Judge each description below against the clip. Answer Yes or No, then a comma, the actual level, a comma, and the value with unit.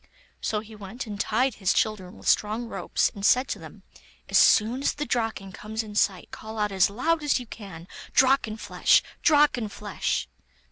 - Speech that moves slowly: No, average, 175 wpm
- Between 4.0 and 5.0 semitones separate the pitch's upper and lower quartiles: No, average, 3.4 semitones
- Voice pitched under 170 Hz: No, high, 215 Hz